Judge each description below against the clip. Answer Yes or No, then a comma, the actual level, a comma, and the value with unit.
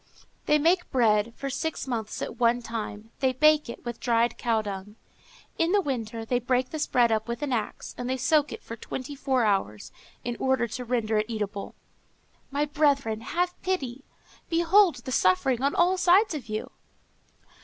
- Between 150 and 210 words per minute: Yes, average, 180 wpm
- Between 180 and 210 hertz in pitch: No, very high, 250 Hz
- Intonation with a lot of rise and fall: No, average, 4.6 semitones